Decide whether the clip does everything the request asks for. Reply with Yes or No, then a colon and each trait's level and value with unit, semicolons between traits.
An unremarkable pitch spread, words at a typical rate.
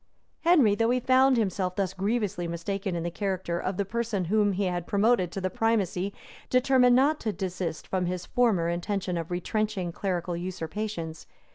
Yes: average, 3.9 semitones; average, 170 wpm